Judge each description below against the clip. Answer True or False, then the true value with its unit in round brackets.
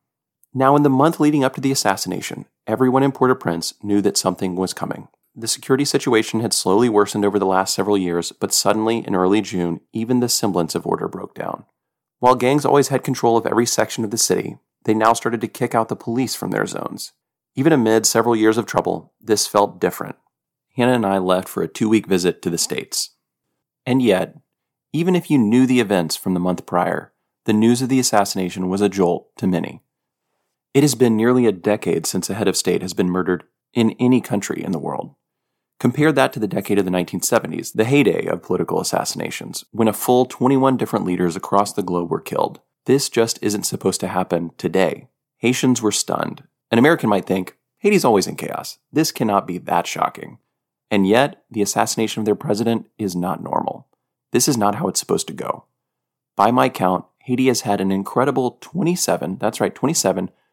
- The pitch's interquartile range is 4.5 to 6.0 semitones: True (4.8 semitones)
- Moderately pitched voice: False (110 Hz)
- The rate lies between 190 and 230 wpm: True (200 wpm)